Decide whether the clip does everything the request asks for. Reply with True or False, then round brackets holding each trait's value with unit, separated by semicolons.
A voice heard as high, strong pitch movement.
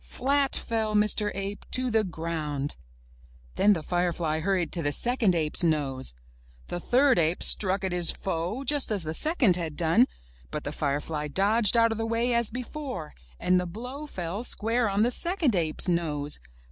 True (195 Hz; 6.3 semitones)